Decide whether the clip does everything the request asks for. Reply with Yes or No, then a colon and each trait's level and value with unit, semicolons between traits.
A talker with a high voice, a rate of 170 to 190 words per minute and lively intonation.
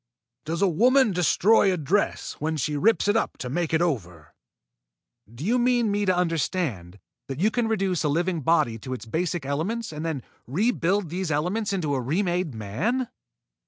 No: medium, 175 Hz; average, 180 wpm; wide, 6.0 semitones